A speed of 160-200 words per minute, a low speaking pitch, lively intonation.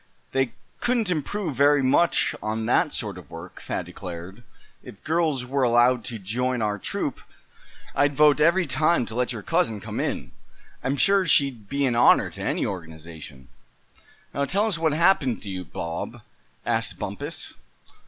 Yes: average, 165 wpm; low, 130 Hz; wide, 6.6 semitones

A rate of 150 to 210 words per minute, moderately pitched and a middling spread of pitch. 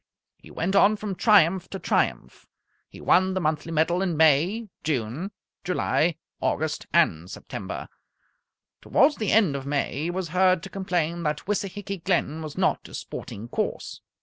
Yes: average, 155 wpm; medium, 175 Hz; average, 3.9 semitones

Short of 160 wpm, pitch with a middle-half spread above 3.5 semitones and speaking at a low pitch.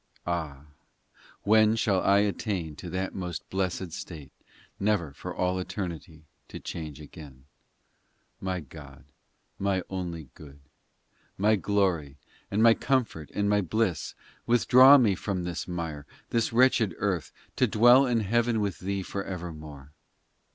Yes: slow, 135 wpm; average, 4.6 semitones; very low, 95 Hz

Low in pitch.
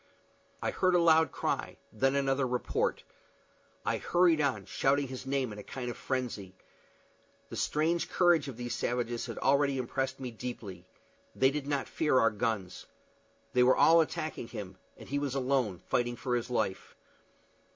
Yes: low, 130 Hz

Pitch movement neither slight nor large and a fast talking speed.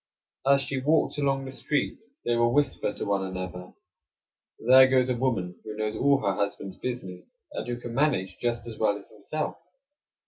No: average, 4.9 semitones; average, 180 wpm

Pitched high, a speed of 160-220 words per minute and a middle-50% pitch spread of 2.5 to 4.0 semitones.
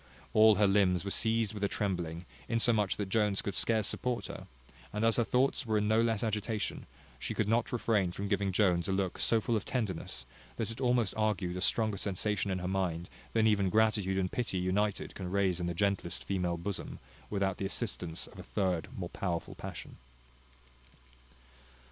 No: low, 100 Hz; average, 190 wpm; average, 3.0 semitones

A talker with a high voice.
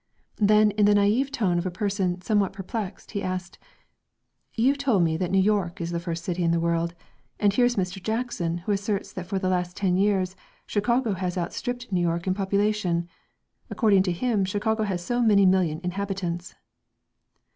Yes: high, 195 Hz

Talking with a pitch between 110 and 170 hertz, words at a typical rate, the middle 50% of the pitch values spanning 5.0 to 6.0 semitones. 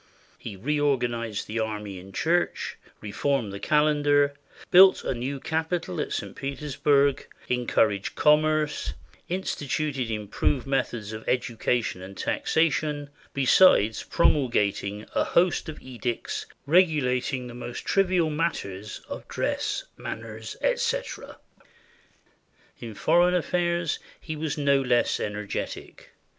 No: low, 135 Hz; slow, 110 wpm; wide, 5.6 semitones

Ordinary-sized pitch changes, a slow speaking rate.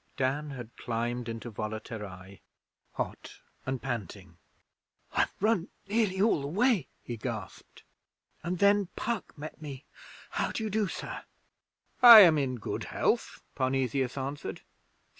No: wide, 8.2 semitones; slow, 130 wpm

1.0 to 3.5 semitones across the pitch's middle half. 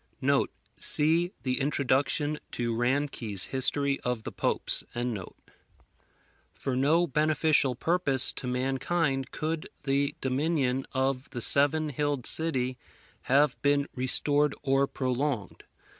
Yes: narrow, 2.5 semitones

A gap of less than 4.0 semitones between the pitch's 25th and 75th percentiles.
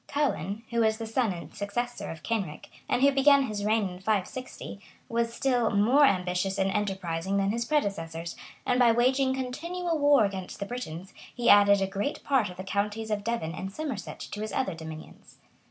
No: average, 4.5 semitones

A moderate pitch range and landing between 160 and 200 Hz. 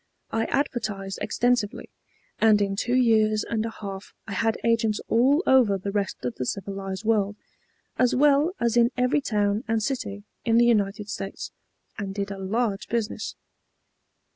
No: average, 3.0 semitones; high, 215 Hz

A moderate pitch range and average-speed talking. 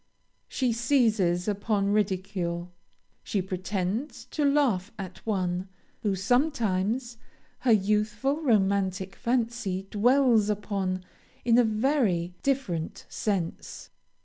No: average, 4.2 semitones; slow, 95 wpm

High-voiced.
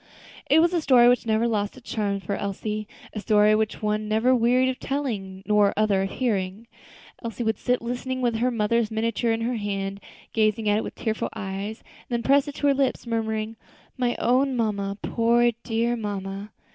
Yes: high, 225 Hz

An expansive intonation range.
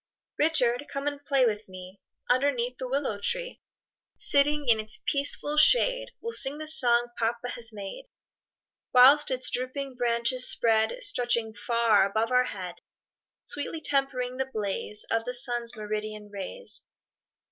No: average, 4.1 semitones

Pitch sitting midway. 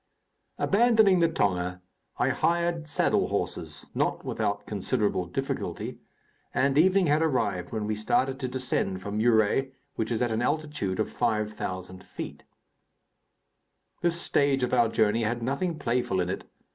No: low, 120 Hz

